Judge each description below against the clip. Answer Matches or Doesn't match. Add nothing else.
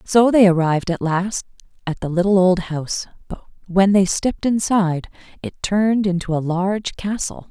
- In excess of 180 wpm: Doesn't match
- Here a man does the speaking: Doesn't match